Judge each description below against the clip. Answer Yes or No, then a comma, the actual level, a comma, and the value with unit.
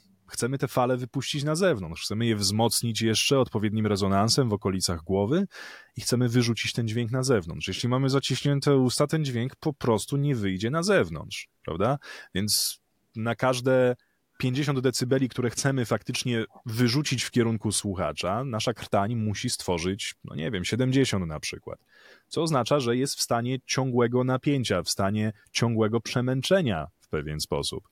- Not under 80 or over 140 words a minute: No, average, 155 wpm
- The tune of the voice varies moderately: Yes, average, 3.6 semitones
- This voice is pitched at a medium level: No, low, 120 Hz